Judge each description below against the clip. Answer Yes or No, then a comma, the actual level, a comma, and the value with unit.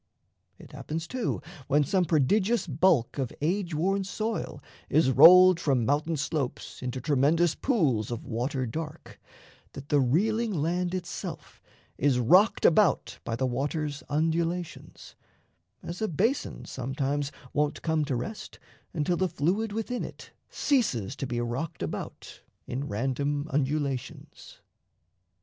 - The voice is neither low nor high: Yes, medium, 150 Hz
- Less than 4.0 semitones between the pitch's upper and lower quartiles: No, average, 5.1 semitones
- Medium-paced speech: No, slow, 130 wpm